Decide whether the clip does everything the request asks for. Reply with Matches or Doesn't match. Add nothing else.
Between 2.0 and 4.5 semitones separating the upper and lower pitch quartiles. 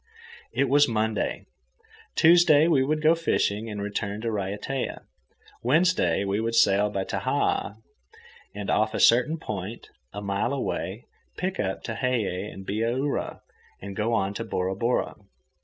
Doesn't match